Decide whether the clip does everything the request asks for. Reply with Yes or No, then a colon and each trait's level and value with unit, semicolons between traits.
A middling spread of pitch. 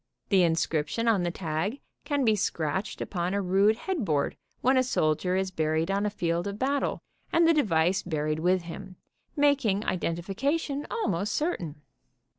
No: wide, 6.4 semitones